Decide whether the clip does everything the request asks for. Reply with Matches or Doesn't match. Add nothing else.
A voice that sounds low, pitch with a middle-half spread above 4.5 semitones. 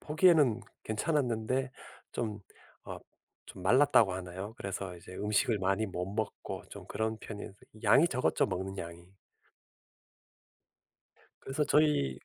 Matches